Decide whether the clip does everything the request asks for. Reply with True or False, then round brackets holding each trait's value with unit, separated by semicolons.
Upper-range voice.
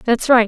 True (235 Hz)